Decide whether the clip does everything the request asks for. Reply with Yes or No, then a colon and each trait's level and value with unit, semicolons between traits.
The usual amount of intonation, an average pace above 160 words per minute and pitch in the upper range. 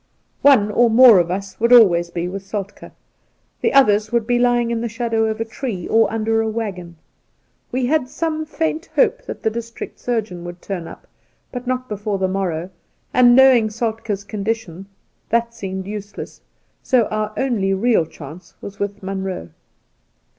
Yes: average, 3.7 semitones; average, 175 wpm; high, 220 Hz